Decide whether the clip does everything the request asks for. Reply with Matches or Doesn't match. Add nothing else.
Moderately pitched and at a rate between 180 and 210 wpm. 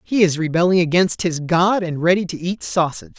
Matches